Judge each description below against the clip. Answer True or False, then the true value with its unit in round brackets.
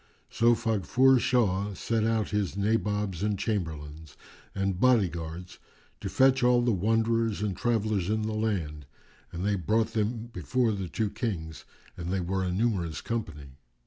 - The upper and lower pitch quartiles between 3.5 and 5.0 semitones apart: True (4.0 semitones)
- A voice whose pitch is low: True (105 Hz)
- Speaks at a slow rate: False (155 wpm)